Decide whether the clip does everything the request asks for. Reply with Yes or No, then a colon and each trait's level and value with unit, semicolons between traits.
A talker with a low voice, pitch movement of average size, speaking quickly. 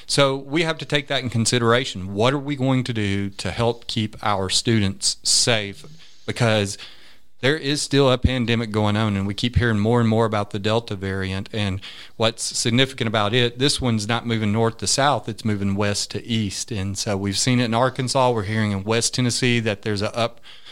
Yes: low, 115 Hz; average, 3.3 semitones; fast, 210 wpm